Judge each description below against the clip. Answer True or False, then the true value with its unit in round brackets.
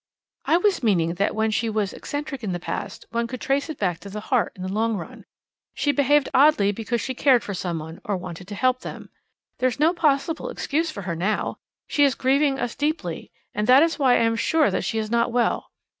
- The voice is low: False (235 Hz)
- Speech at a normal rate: False (225 wpm)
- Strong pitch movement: True (5.8 semitones)